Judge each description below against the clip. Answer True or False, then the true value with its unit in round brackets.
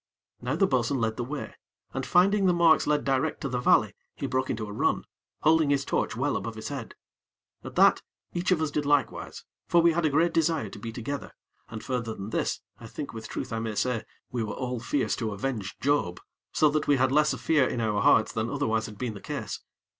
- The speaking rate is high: True (230 wpm)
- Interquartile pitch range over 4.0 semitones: True (5.0 semitones)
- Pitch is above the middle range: False (130 Hz)